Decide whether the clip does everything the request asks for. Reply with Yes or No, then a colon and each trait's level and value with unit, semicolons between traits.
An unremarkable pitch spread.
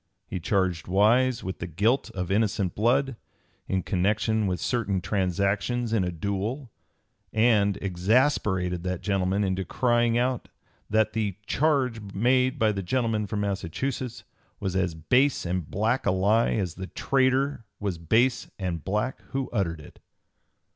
Yes: average, 4.4 semitones